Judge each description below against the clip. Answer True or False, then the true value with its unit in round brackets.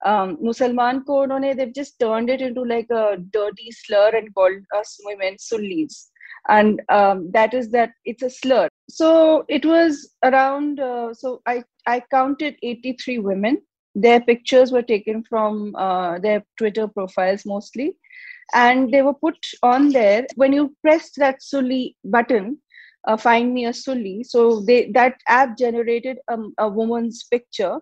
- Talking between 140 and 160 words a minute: True (155 wpm)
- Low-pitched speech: False (240 Hz)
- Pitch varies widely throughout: False (3.6 semitones)